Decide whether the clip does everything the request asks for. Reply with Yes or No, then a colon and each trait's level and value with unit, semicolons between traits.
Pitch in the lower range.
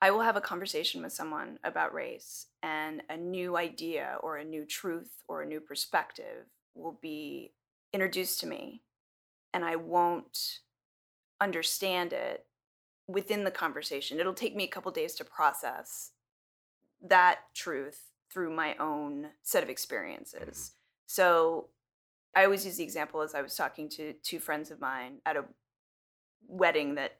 No: medium, 175 Hz